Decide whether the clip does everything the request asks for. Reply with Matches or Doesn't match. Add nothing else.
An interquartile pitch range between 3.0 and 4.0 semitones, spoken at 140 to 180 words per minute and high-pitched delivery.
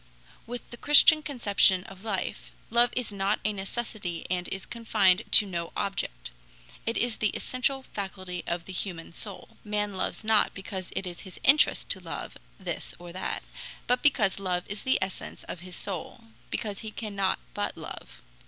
Matches